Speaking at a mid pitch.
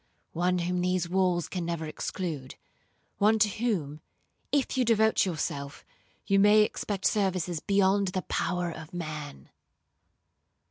Yes: medium, 180 Hz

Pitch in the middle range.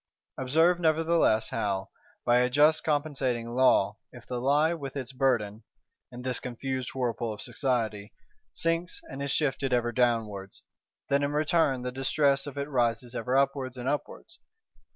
No: low, 130 Hz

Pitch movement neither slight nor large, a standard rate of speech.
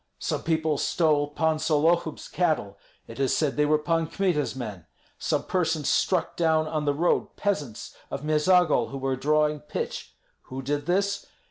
No: narrow, 2.3 semitones; average, 160 wpm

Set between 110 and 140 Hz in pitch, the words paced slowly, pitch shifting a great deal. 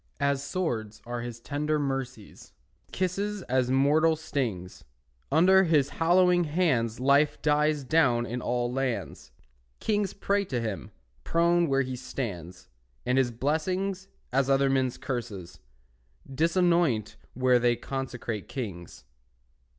No: low, 135 Hz; slow, 125 wpm; average, 5.0 semitones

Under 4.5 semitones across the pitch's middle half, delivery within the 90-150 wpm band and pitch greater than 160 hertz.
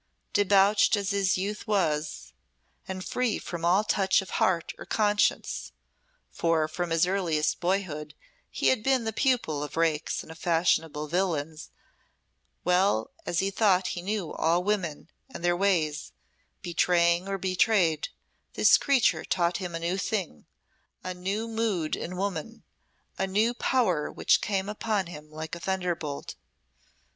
Yes: average, 3.4 semitones; average, 145 wpm; medium, 185 Hz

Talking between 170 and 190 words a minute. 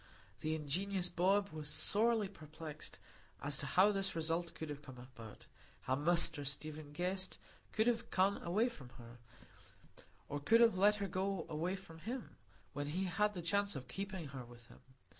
Yes: average, 175 wpm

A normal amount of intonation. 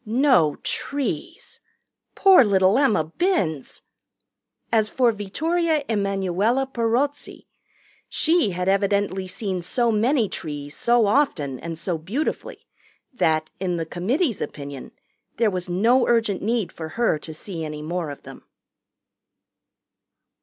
No: wide, 6.1 semitones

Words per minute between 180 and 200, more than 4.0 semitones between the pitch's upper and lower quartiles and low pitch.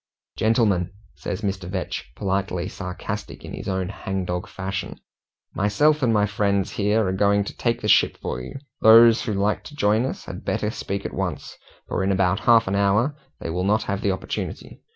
No: average, 190 wpm; narrow, 2.4 semitones; low, 100 Hz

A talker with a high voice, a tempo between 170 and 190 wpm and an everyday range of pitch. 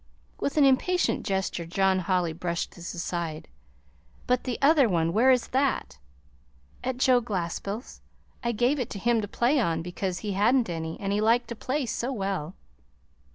No: high, 210 Hz; average, 175 wpm; wide, 6.0 semitones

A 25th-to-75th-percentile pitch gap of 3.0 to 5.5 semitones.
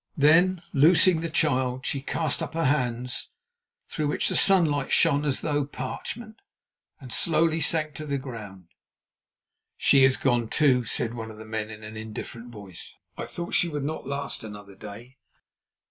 Yes: average, 5.1 semitones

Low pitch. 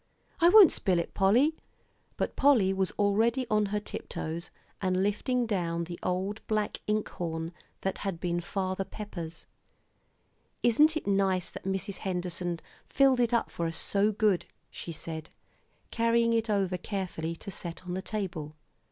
No: high, 195 Hz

